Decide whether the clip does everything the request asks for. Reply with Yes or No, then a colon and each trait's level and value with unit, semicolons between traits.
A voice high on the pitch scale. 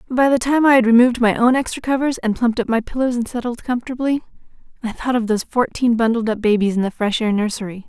Yes: high, 235 Hz